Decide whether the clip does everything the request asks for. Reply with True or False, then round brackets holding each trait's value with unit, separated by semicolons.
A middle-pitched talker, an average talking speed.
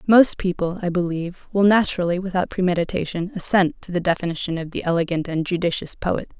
True (180 Hz; 170 wpm)